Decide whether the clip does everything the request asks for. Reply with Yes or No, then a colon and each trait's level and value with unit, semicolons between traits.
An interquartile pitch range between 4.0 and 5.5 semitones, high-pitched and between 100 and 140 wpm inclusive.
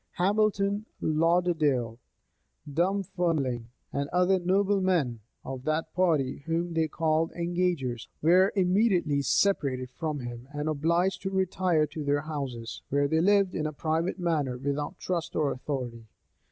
No: average, 4.3 semitones; medium, 160 Hz; slow, 135 wpm